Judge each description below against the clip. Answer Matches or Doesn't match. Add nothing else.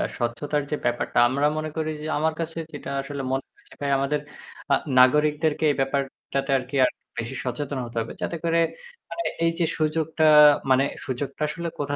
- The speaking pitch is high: Doesn't match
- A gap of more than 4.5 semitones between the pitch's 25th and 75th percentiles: Doesn't match